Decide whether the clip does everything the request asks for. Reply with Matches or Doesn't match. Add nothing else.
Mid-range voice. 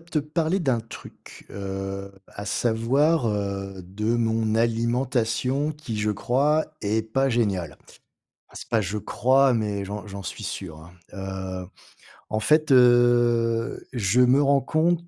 Doesn't match